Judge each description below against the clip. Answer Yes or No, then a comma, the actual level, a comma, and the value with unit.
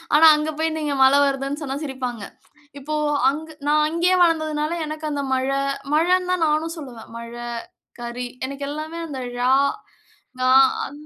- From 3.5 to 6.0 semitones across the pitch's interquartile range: No, average, 2.9 semitones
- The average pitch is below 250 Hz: No, very high, 295 Hz